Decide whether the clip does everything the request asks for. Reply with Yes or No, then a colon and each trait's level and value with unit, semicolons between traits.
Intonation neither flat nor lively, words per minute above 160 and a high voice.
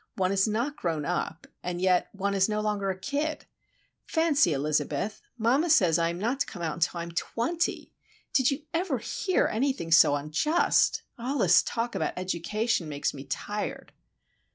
No: wide, 7.5 semitones; average, 175 wpm; high, 200 Hz